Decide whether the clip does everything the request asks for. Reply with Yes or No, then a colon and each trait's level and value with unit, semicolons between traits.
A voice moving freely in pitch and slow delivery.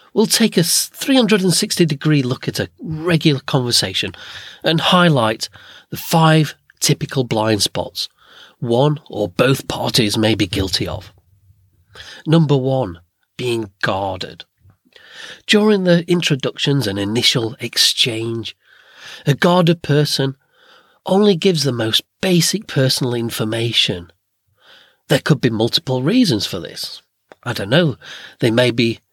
Yes: wide, 7.1 semitones; slow, 120 wpm